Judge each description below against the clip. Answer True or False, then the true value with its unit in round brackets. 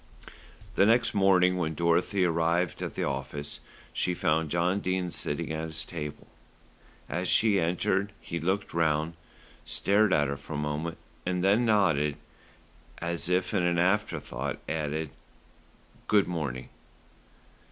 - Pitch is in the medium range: False (85 Hz)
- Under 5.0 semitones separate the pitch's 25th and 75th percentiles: True (3.2 semitones)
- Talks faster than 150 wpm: False (140 wpm)